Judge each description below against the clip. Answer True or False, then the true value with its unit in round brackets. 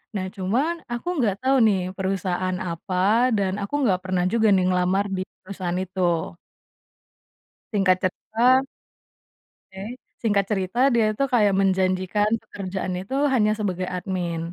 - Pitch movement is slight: True (2.3 semitones)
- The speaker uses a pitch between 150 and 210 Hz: True (190 Hz)